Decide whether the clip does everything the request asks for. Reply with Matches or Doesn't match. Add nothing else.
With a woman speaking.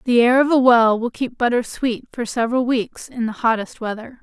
Matches